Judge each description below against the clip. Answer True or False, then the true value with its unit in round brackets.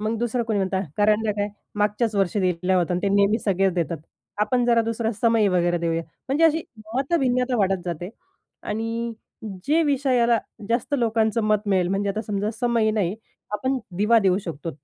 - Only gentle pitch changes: False (3.6 semitones)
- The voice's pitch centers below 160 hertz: False (215 Hz)